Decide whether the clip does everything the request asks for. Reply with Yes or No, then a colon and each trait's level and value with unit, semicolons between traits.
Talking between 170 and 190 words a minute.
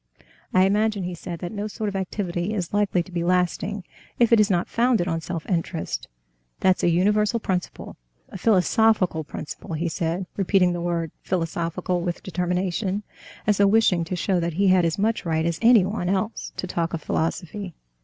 Yes: average, 185 wpm